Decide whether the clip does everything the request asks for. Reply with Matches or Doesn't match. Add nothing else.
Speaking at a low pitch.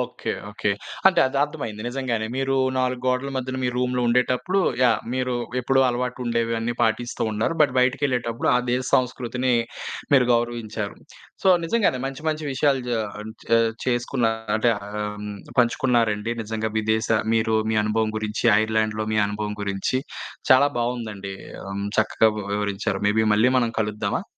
Matches